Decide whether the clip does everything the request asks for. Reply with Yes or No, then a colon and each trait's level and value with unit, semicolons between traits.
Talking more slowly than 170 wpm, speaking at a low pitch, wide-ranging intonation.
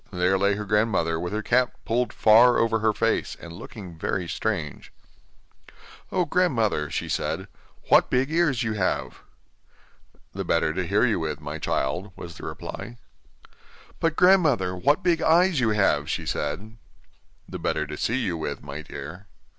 Yes: average, 160 wpm; low, 105 Hz; wide, 6.0 semitones